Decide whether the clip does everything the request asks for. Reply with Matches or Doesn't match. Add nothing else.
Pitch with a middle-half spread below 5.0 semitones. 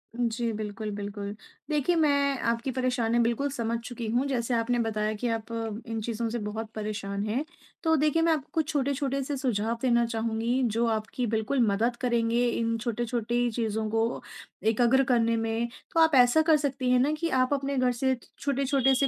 Matches